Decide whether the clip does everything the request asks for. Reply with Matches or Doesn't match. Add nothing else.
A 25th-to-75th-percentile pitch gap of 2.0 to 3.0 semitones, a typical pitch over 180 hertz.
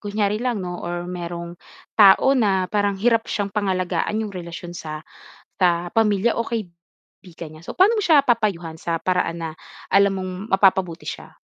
Doesn't match